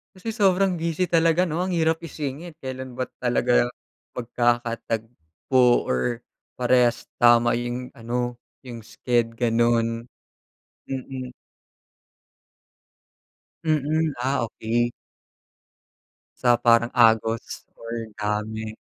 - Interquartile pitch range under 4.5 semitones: Yes, average, 3.9 semitones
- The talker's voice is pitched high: No, low, 120 Hz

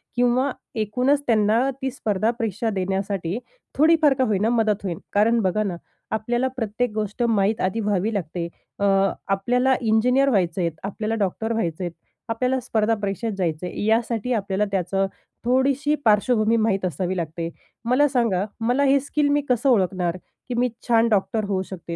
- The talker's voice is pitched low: No, high, 220 Hz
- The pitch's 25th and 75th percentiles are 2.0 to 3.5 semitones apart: No, average, 4.1 semitones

